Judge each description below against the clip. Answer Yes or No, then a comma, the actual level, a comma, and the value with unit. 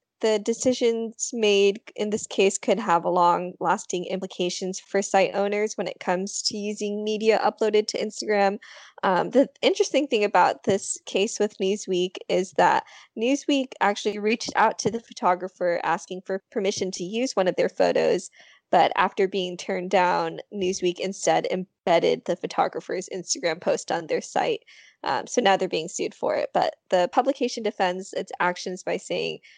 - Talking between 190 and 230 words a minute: No, average, 165 wpm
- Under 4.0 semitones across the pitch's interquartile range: Yes, average, 3.1 semitones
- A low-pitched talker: No, high, 200 Hz